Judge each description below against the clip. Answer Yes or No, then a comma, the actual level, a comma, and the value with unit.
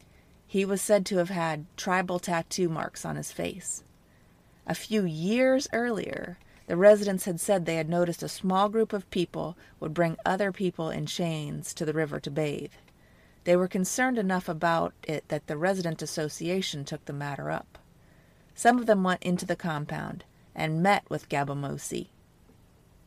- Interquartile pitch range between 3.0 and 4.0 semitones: Yes, average, 3.6 semitones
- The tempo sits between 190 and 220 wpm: No, average, 165 wpm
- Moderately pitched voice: Yes, medium, 175 Hz